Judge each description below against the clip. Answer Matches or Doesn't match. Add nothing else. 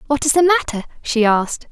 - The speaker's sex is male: Doesn't match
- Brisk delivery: Matches